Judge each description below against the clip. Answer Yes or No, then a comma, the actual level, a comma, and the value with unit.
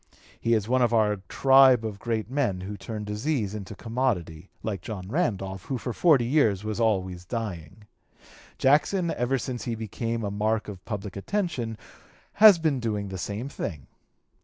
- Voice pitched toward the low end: Yes, low, 110 Hz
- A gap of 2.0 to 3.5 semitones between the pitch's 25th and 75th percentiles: No, average, 4.2 semitones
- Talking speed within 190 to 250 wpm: No, average, 165 wpm